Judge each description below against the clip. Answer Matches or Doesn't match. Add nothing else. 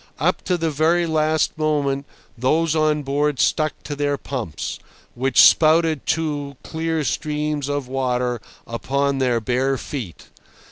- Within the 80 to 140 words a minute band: Matches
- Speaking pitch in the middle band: Matches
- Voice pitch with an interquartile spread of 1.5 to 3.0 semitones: Matches